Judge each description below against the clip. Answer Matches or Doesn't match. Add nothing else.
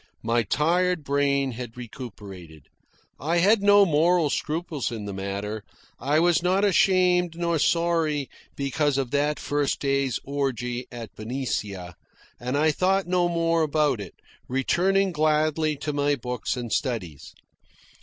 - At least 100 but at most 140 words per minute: Matches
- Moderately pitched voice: Matches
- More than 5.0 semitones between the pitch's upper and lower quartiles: Matches